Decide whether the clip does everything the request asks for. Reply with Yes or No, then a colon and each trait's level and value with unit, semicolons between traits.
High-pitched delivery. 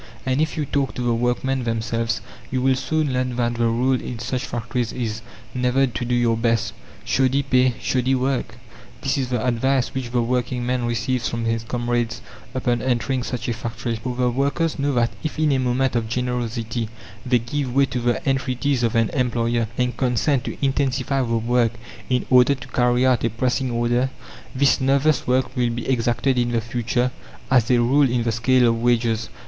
No: low, 125 Hz